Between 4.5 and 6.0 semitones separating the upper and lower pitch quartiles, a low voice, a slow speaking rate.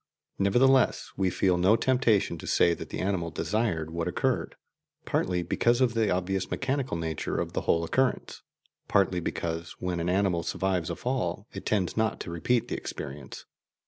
No: average, 5.1 semitones; very low, 95 Hz; average, 170 wpm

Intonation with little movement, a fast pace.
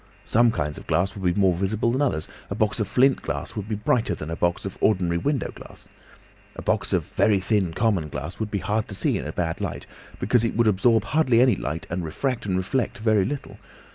No: average, 4.5 semitones; fast, 230 wpm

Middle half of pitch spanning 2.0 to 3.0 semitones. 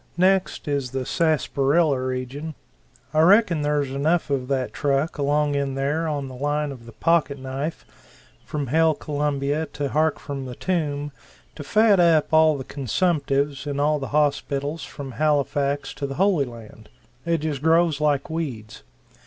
Yes: narrow, 2.5 semitones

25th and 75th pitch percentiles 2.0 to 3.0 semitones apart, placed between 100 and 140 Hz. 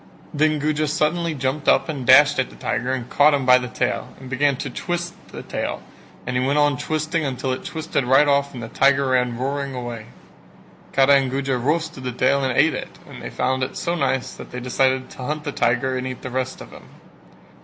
Yes: narrow, 2.6 semitones; low, 135 Hz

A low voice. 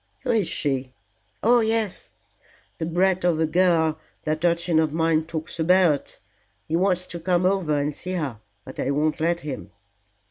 No: medium, 165 Hz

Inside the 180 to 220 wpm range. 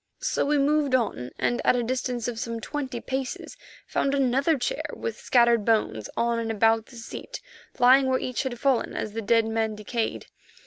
Yes: average, 185 wpm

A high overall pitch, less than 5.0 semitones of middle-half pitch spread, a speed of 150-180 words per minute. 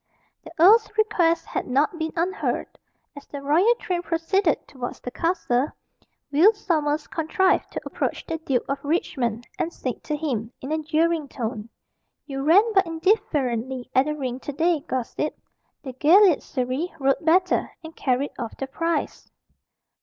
Yes: very high, 305 Hz; average, 4.2 semitones; average, 155 wpm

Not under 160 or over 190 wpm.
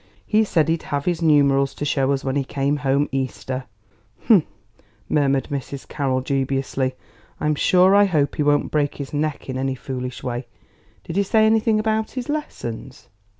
Yes: average, 175 wpm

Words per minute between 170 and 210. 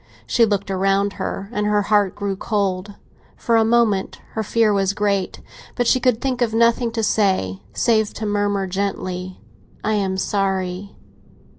No: average, 160 wpm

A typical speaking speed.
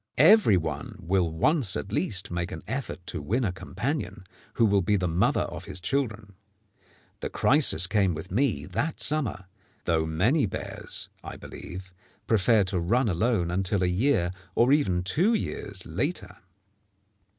Yes: average, 155 wpm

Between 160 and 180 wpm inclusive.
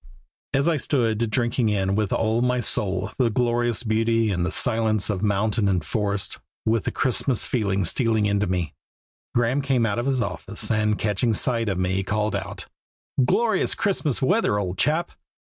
Yes: average, 170 wpm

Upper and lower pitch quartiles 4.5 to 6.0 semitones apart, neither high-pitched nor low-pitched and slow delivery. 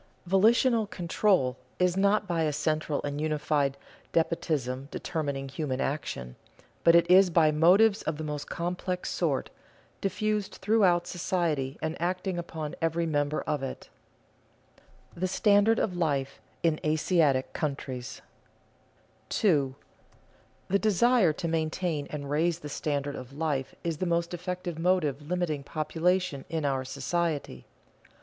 No: average, 3.8 semitones; medium, 160 Hz; slow, 130 wpm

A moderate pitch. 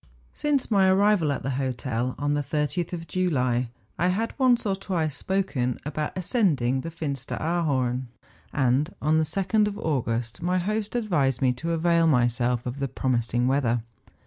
Yes: medium, 150 Hz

